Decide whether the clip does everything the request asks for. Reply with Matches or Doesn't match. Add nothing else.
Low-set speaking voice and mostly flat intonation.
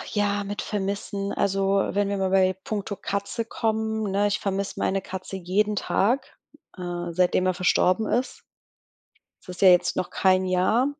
Doesn't match